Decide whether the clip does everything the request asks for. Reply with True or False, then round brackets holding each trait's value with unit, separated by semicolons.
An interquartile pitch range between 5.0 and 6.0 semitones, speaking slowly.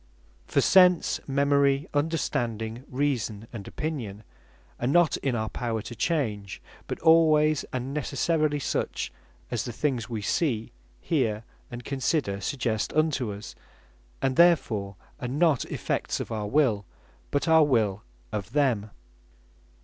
True (5.4 semitones; 130 wpm)